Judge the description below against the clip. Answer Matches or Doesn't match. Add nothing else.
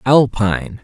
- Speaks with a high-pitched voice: Doesn't match